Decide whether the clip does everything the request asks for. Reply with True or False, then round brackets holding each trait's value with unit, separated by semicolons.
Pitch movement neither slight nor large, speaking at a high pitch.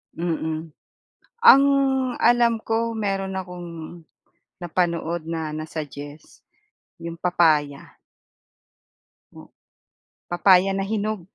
False (3.5 semitones; 175 Hz)